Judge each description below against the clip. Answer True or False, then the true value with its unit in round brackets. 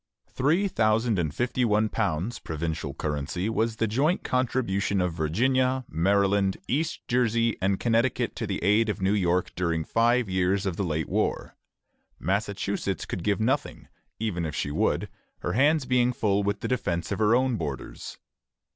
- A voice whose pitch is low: True (105 Hz)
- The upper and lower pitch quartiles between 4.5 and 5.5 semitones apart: True (5.1 semitones)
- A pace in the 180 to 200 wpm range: False (165 wpm)